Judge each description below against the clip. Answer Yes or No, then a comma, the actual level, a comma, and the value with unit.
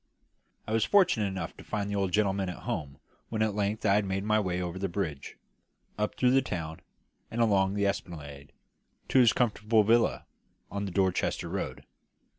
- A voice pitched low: Yes, low, 100 Hz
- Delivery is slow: No, average, 185 wpm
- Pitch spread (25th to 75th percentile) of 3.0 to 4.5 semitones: No, narrow, 2.6 semitones